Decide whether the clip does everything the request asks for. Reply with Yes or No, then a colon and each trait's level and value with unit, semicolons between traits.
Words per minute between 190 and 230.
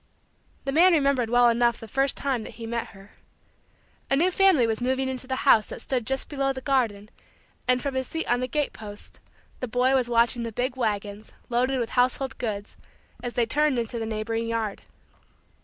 Yes: average, 200 wpm